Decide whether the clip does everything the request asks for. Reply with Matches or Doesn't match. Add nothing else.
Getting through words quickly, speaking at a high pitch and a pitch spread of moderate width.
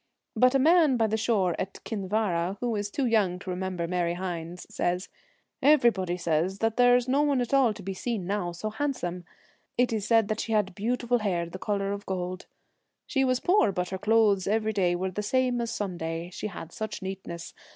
Matches